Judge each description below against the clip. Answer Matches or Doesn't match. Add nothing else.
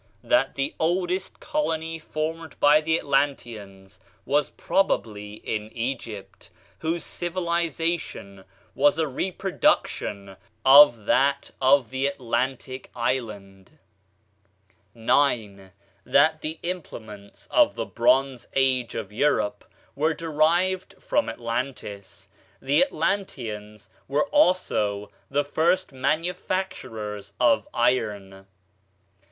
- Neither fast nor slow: Doesn't match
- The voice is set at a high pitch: Doesn't match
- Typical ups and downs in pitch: Doesn't match